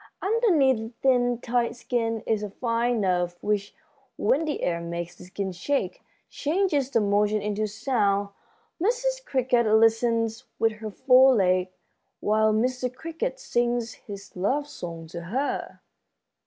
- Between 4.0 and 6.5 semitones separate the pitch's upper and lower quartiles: Yes, average, 4.3 semitones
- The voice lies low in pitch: No, high, 230 Hz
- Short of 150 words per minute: Yes, average, 140 wpm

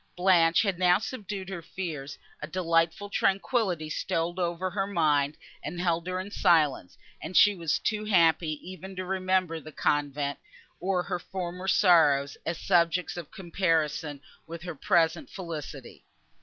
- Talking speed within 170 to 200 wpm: No, average, 145 wpm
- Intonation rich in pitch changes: No, average, 2.7 semitones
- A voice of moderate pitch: Yes, medium, 175 Hz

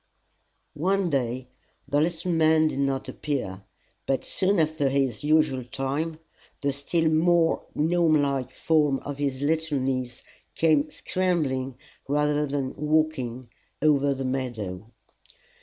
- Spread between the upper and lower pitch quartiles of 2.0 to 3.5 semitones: Yes, average, 3.0 semitones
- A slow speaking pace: Yes, slow, 125 wpm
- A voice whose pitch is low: No, medium, 145 Hz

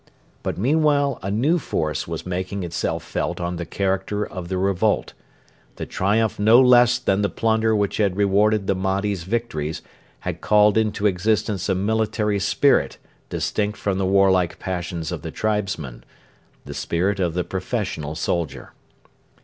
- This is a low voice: Yes, low, 100 Hz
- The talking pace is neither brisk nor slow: Yes, average, 150 wpm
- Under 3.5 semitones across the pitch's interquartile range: Yes, average, 3.0 semitones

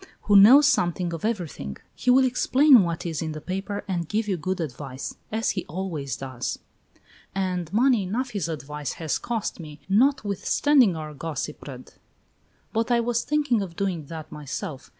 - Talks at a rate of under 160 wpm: No, average, 165 wpm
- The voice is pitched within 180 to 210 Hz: Yes, medium, 185 Hz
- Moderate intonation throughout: No, wide, 6.7 semitones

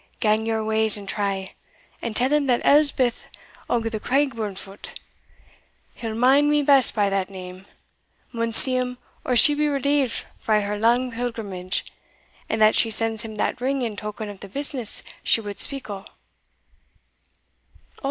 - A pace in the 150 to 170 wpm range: Yes, average, 155 wpm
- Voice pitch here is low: No, high, 225 Hz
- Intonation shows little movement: No, average, 3.7 semitones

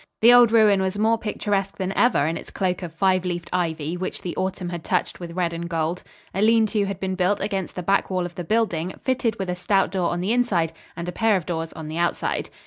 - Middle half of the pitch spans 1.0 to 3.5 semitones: Yes, average, 3.0 semitones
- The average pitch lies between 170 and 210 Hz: Yes, medium, 185 Hz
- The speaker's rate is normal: No, fast, 250 wpm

